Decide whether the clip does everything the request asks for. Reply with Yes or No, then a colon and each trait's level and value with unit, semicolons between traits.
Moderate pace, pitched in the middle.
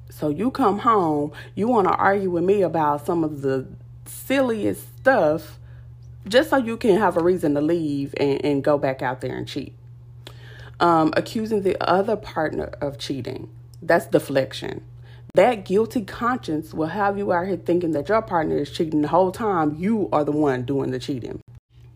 Yes: average, 180 wpm; medium, 150 Hz